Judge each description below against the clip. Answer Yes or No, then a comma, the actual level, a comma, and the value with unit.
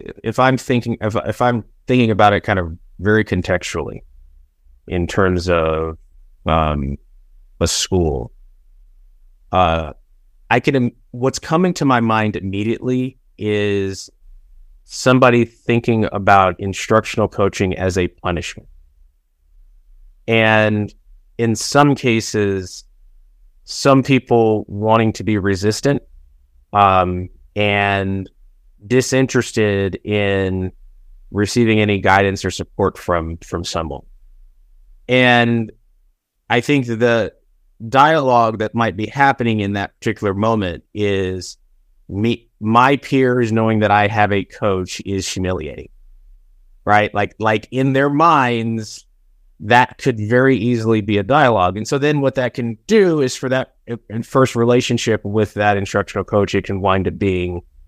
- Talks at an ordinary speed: No, slow, 125 wpm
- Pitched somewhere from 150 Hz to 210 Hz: No, low, 100 Hz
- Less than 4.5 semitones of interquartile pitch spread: No, average, 5.0 semitones